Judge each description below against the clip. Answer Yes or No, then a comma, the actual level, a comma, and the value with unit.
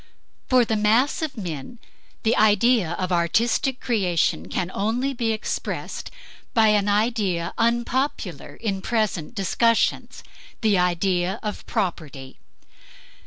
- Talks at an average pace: No, slow, 115 wpm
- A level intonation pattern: No, average, 4.6 semitones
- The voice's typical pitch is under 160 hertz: No, high, 210 Hz